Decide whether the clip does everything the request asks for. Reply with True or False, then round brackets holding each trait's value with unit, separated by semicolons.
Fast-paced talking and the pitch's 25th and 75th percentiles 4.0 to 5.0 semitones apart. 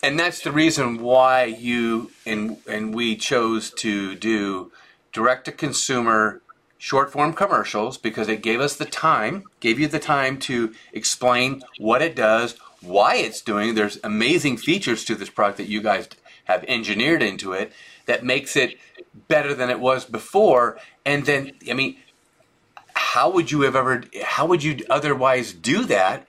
False (165 wpm; 4.7 semitones)